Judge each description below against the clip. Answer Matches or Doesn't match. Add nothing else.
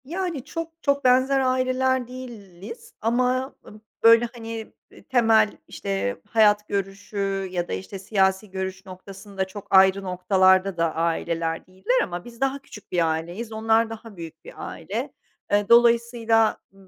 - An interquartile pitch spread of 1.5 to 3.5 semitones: Doesn't match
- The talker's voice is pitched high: Matches